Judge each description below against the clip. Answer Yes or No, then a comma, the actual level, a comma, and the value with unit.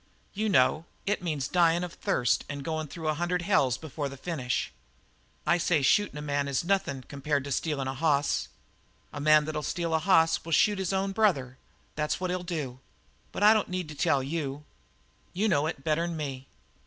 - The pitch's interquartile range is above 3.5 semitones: Yes, average, 3.9 semitones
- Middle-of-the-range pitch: Yes, medium, 155 Hz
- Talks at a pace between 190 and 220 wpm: Yes, average, 195 wpm